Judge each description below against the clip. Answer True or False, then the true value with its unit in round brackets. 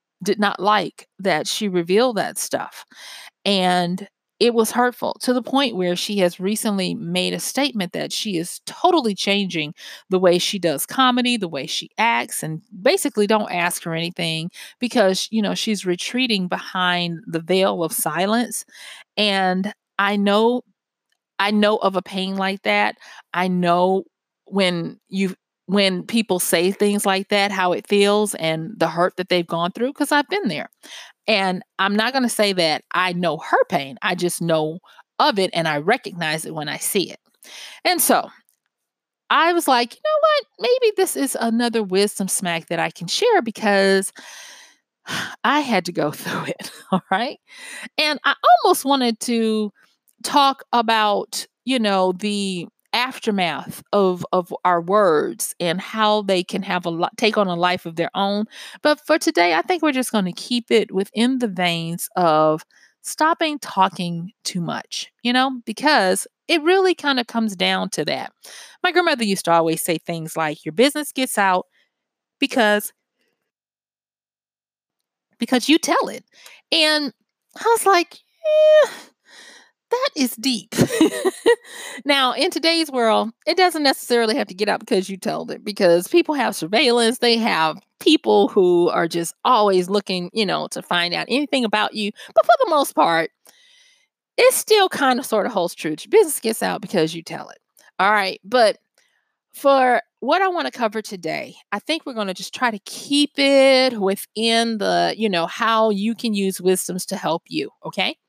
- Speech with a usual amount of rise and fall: False (6.2 semitones)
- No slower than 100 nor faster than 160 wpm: False (170 wpm)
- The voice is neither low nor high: False (210 Hz)